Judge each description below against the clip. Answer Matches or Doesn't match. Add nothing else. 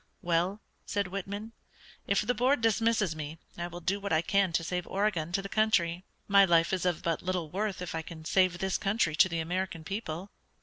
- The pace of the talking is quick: Matches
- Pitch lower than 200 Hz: Matches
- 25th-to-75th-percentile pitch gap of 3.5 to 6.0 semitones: Doesn't match